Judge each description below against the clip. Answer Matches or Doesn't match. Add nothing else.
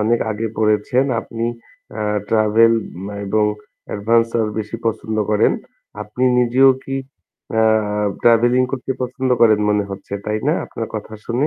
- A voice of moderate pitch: Doesn't match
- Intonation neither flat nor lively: Doesn't match